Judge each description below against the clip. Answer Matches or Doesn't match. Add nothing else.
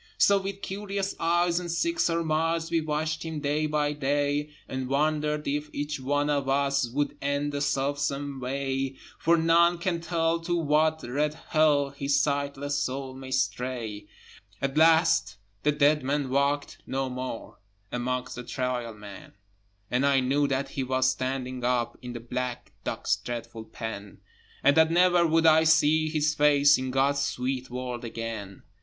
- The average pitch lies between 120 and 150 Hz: Matches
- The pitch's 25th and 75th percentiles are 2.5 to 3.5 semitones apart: Matches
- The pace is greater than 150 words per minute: Matches